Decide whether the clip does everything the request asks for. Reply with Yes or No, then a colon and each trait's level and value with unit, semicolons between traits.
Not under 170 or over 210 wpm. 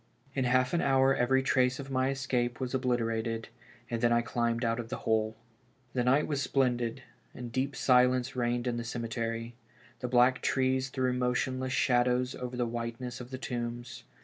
Yes: average, 175 wpm